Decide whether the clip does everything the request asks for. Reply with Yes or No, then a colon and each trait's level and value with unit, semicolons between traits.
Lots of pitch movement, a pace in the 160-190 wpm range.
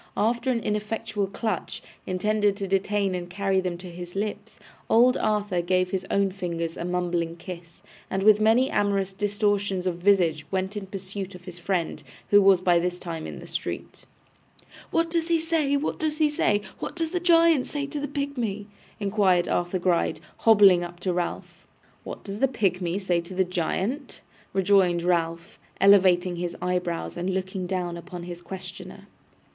No: average, 3.0 semitones; average, 175 wpm